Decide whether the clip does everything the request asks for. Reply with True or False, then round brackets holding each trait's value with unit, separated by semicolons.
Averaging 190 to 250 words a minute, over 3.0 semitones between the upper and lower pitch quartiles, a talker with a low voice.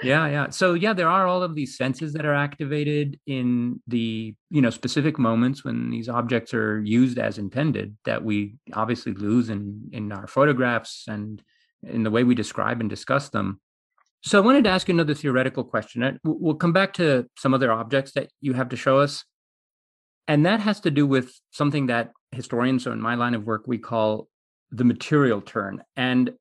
True (195 wpm; 4.5 semitones; 125 Hz)